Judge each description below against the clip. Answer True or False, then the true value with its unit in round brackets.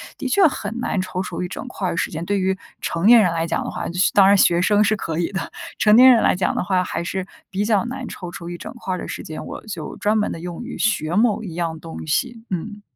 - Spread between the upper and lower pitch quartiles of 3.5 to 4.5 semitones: True (3.9 semitones)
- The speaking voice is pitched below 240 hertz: True (190 Hz)